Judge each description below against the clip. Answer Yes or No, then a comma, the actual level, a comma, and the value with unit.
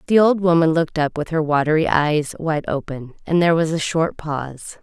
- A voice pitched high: No, medium, 160 Hz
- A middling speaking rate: No, fast, 210 wpm